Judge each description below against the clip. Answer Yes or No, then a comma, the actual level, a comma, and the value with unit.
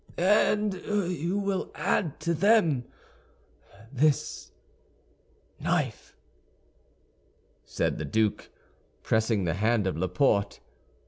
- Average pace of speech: No, slow, 85 wpm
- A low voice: No, medium, 150 Hz